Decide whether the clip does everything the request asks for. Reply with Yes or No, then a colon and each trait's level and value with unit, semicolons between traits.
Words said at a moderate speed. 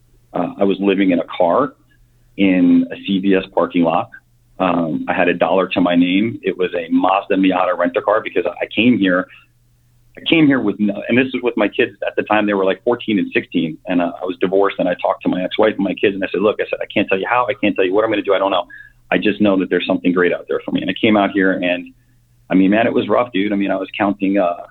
No: fast, 285 wpm